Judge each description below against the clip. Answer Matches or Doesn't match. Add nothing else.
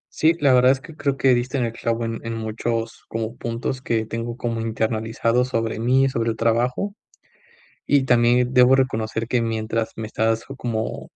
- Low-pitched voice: Matches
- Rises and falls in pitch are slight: Matches